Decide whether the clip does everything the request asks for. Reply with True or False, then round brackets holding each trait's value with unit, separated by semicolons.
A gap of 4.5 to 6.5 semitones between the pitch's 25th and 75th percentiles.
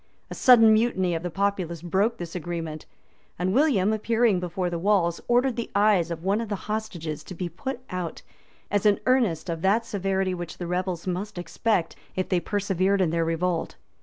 False (3.6 semitones)